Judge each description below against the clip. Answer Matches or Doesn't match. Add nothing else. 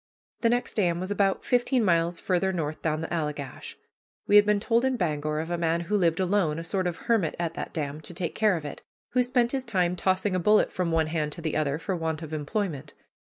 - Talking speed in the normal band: Doesn't match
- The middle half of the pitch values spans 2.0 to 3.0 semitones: Doesn't match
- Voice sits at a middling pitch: Matches